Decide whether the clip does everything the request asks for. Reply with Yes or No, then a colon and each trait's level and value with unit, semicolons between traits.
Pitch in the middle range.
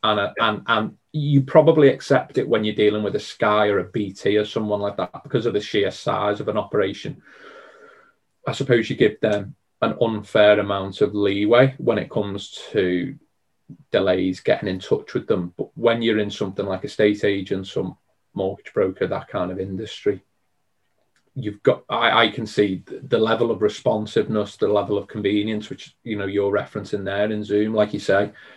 No: low, 105 Hz